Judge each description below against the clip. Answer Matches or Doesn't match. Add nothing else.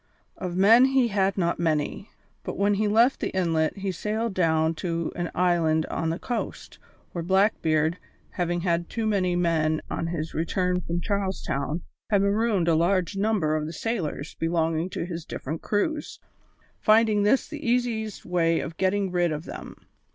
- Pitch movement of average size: Matches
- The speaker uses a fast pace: Doesn't match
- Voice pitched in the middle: Matches